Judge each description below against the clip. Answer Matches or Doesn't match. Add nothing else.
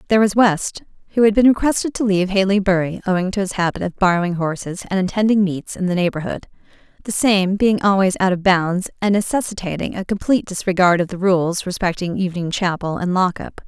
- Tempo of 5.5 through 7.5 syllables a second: Matches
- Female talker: Matches